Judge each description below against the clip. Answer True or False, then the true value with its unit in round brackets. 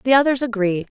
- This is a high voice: True (235 Hz)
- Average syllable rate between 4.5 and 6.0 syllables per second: False (6.3 syllables/s)